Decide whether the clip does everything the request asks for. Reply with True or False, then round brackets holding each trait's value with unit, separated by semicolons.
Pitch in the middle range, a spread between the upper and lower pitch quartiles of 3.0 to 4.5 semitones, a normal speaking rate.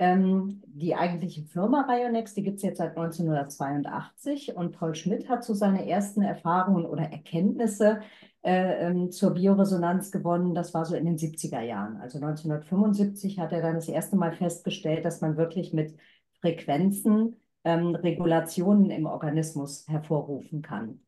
True (175 Hz; 3.3 semitones; 145 wpm)